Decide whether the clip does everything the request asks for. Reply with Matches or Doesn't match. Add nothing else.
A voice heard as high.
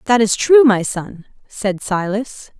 Matches